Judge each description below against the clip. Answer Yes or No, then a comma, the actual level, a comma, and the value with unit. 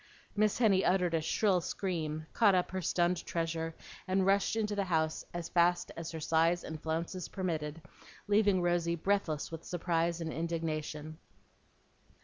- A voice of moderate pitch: Yes, medium, 170 Hz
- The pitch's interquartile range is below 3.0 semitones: Yes, narrow, 2.5 semitones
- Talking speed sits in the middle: Yes, average, 150 wpm